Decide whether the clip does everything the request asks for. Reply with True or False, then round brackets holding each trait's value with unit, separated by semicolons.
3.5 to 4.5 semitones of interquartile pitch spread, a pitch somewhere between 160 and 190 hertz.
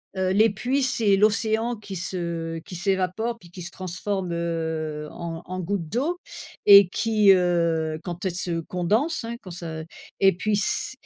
True (3.9 semitones; 185 Hz)